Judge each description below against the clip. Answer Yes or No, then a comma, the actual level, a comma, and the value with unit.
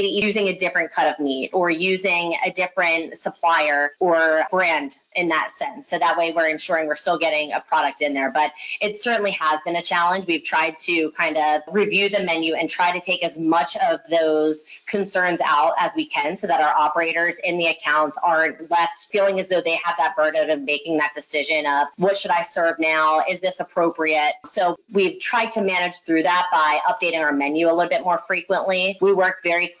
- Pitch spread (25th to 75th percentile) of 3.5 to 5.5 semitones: No, average, 2.9 semitones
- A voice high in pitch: No, medium, 170 Hz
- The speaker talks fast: Yes, fast, 210 wpm